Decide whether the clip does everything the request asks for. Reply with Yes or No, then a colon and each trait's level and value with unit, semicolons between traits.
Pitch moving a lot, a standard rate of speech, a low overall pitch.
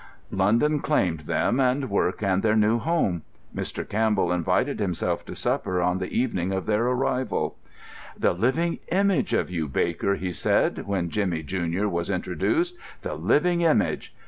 Yes: wide, 6.5 semitones; average, 155 wpm; low, 100 Hz